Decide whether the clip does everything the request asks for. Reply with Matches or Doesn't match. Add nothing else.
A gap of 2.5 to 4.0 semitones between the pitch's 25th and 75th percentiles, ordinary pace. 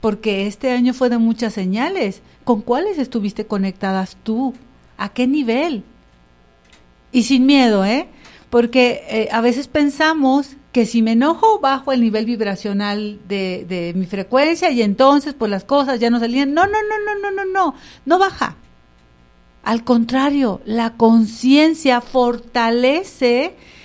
Doesn't match